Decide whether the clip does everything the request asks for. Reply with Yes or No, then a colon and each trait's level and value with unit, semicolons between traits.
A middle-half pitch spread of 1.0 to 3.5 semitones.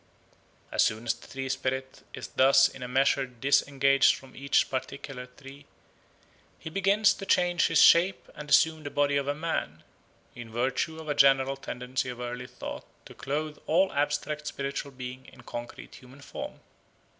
Yes: narrow, 2.5 semitones